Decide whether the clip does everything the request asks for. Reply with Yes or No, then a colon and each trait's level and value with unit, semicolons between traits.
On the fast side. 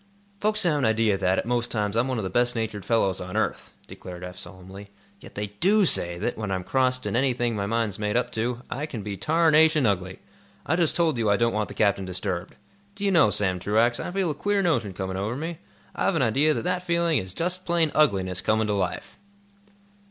Yes: fast, 225 wpm